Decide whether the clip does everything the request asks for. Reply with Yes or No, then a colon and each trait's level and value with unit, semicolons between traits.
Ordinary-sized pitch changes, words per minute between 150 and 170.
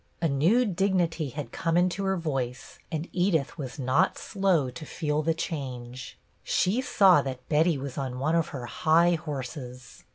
Yes: average, 4.7 semitones; average, 165 wpm